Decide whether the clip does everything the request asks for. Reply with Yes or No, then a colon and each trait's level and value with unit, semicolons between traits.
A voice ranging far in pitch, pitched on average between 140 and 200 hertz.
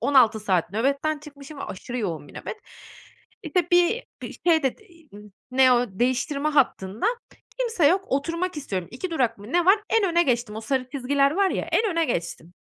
No: wide, 6.0 semitones; very high, 275 Hz